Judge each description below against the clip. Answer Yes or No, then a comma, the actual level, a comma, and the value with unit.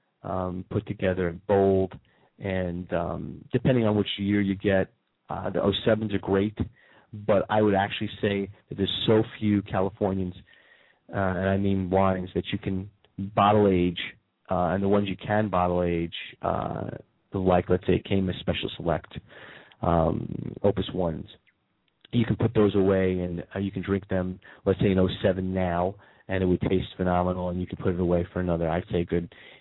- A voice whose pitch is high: No, very low, 95 Hz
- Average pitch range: No, narrow, 2.0 semitones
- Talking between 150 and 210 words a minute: Yes, average, 180 wpm